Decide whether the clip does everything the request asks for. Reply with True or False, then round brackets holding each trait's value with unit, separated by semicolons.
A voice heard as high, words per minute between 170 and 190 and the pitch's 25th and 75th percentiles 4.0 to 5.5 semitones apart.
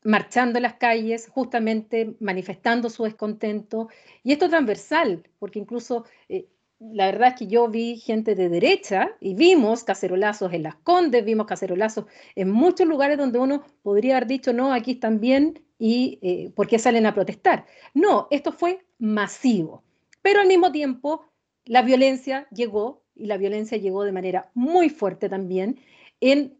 False (235 Hz; 160 wpm; 4.8 semitones)